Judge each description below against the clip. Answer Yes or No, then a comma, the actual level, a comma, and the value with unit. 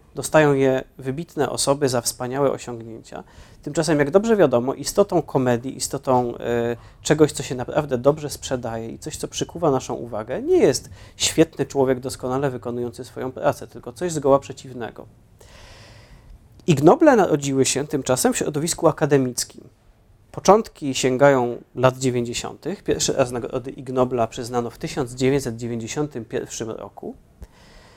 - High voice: No, low, 130 Hz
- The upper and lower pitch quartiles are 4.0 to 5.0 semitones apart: No, average, 3.3 semitones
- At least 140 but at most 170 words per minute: No, average, 125 wpm